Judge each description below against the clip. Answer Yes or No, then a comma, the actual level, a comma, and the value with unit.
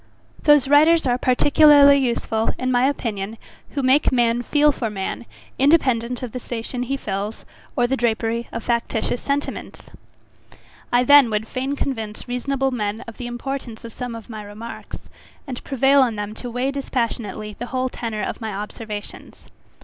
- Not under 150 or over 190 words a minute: Yes, average, 165 wpm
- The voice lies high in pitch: Yes, high, 245 Hz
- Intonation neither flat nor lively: Yes, average, 3.2 semitones